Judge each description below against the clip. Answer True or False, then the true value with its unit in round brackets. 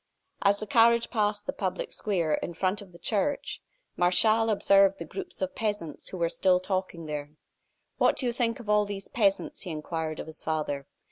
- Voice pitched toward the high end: True (195 Hz)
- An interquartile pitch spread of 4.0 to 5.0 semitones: True (4.3 semitones)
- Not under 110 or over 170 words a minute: False (195 wpm)